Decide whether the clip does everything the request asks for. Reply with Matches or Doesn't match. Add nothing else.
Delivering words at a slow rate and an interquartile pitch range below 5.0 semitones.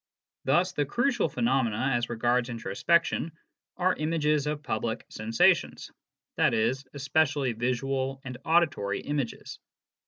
Matches